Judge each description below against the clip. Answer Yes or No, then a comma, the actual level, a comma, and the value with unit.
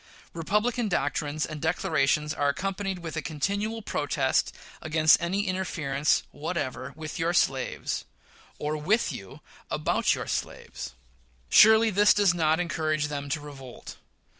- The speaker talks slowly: Yes, slow, 130 wpm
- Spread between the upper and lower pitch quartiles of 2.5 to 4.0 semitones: No, average, 4.6 semitones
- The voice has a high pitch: No, medium, 160 Hz